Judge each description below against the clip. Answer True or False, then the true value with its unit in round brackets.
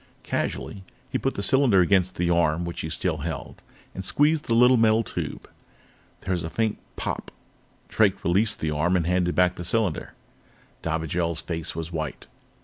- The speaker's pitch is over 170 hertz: False (90 Hz)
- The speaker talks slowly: False (170 wpm)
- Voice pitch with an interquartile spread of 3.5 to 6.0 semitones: True (4.3 semitones)